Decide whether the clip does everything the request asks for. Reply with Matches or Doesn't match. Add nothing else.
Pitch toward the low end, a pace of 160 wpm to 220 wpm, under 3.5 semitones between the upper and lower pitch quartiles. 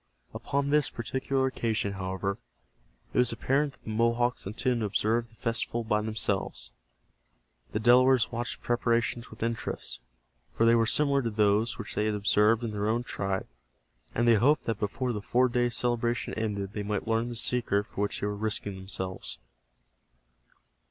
Matches